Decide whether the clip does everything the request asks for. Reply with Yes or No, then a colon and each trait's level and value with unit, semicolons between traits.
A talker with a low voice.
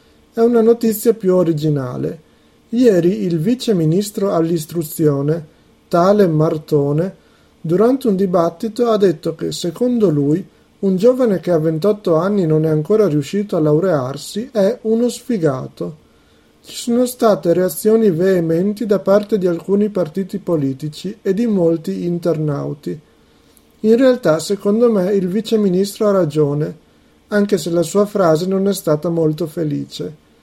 No: medium, 185 Hz